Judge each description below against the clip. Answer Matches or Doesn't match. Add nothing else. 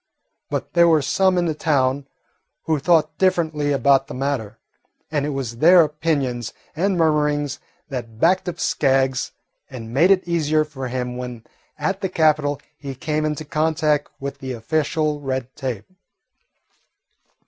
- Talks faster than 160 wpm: Doesn't match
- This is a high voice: Doesn't match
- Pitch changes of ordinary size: Matches